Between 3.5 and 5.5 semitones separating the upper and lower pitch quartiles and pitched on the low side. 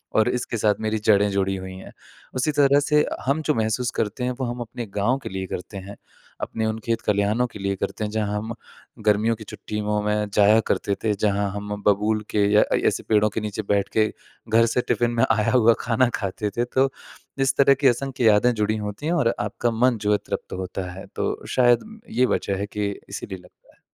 No: average, 2.8 semitones; low, 110 Hz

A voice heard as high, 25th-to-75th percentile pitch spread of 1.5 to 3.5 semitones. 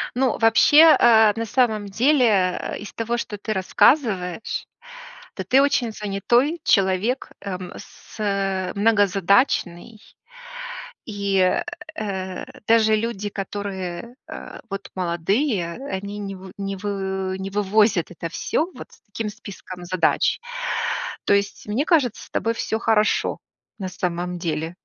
Yes: high, 200 Hz; average, 3.2 semitones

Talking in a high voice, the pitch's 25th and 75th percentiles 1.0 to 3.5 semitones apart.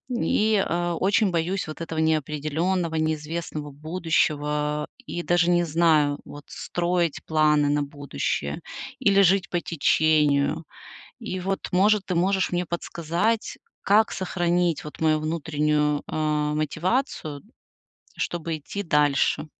No: medium, 160 Hz; average, 2.9 semitones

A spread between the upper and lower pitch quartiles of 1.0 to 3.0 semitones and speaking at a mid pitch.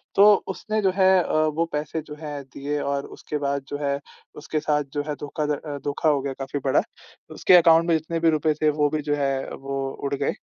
Yes: narrow, 2.5 semitones; medium, 150 Hz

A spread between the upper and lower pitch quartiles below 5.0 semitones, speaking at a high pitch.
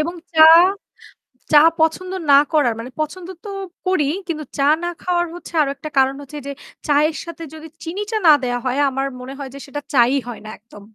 Yes: average, 3.7 semitones; very high, 295 Hz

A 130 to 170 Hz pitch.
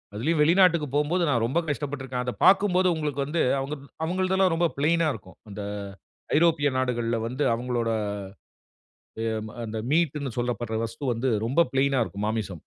Yes: medium, 140 Hz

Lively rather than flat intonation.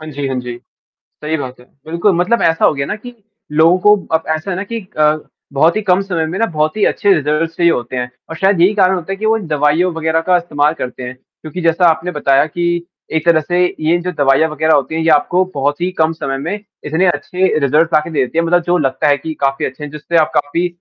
No: average, 3.3 semitones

